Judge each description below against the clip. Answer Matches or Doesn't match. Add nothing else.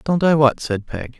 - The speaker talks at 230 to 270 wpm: Matches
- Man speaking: Matches